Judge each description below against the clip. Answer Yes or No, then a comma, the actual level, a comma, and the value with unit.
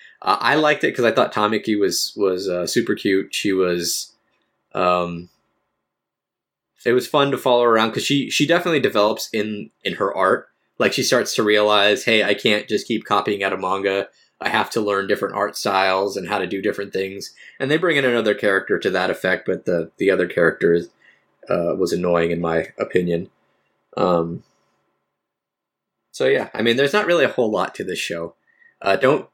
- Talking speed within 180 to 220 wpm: Yes, average, 190 wpm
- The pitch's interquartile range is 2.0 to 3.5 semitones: No, average, 4.5 semitones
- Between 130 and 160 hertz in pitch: No, low, 105 Hz